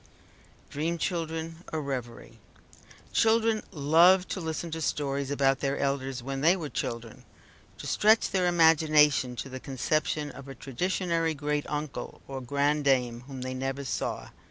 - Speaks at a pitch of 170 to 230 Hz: No, medium, 145 Hz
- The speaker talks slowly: No, average, 145 wpm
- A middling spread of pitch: Yes, average, 3.3 semitones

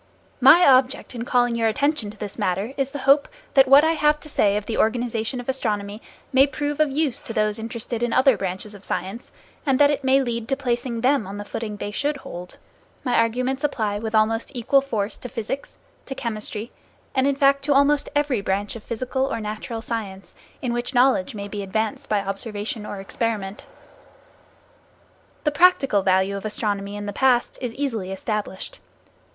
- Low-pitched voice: No, high, 235 Hz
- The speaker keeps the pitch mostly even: No, average, 4.5 semitones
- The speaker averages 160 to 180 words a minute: No, average, 190 wpm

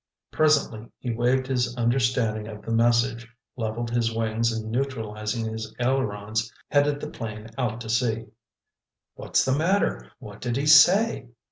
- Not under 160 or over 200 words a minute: No, average, 145 wpm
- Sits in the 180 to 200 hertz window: No, low, 115 Hz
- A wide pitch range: No, average, 2.9 semitones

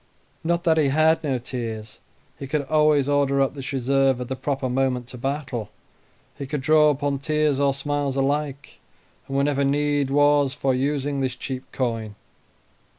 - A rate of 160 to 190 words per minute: Yes, average, 165 wpm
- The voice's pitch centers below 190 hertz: Yes, medium, 140 Hz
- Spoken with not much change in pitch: Yes, narrow, 1.8 semitones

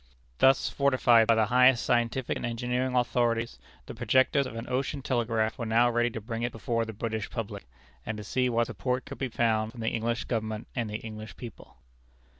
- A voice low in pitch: Yes, low, 115 Hz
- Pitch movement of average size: No, narrow, 2.0 semitones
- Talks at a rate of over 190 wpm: Yes, average, 200 wpm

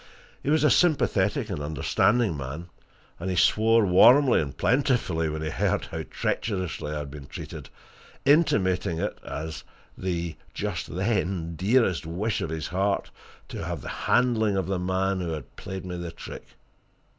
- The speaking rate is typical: Yes, average, 165 wpm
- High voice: No, very low, 95 Hz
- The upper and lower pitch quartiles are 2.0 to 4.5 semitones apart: No, average, 5.1 semitones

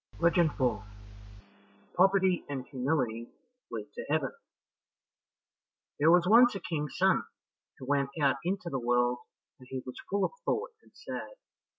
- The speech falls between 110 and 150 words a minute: Yes, average, 145 wpm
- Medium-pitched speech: Yes, medium, 145 Hz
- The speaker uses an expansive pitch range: Yes, wide, 5.9 semitones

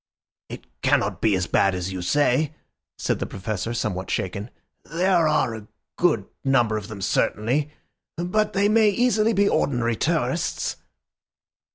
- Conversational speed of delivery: Yes, average, 145 wpm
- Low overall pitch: Yes, low, 120 Hz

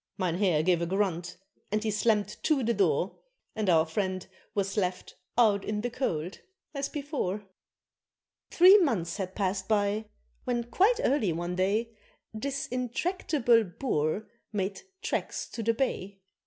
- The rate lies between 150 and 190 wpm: No, average, 140 wpm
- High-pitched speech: Yes, high, 210 Hz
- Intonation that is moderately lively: Yes, average, 4.4 semitones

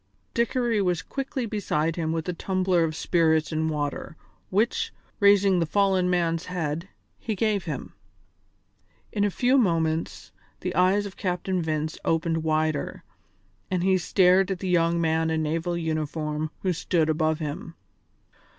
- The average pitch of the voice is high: No, medium, 170 Hz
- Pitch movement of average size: Yes, average, 3.2 semitones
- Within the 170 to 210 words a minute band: No, average, 150 wpm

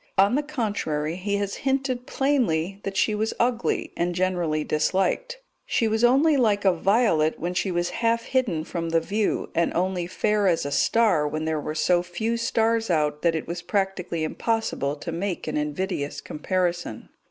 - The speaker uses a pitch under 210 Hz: Yes, medium, 185 Hz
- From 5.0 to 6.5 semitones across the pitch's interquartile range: Yes, wide, 5.4 semitones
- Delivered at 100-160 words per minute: No, average, 175 wpm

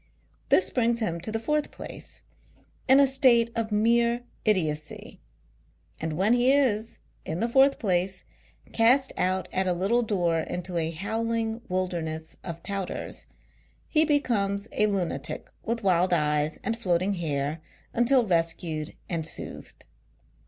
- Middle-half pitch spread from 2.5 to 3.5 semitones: No, wide, 5.5 semitones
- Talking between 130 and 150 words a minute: Yes, average, 140 wpm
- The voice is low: No, high, 200 Hz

